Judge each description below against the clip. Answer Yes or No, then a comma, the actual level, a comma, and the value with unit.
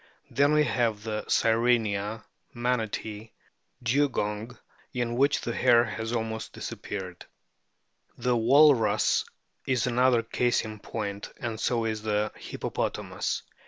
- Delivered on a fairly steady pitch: Yes, narrow, 2.3 semitones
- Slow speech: Yes, slow, 115 wpm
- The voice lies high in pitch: No, low, 115 Hz